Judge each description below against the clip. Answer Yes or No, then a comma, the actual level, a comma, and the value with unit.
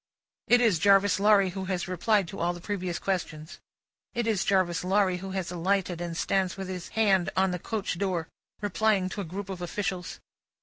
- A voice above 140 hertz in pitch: Yes, high, 190 Hz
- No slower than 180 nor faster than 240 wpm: Yes, average, 190 wpm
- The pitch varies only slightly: Yes, narrow, 2.2 semitones